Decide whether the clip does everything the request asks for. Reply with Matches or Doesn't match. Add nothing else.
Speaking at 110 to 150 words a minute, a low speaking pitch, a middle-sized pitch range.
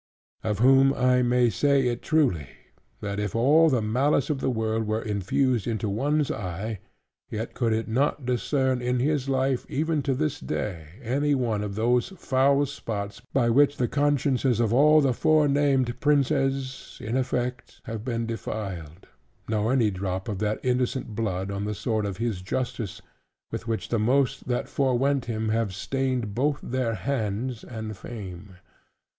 Doesn't match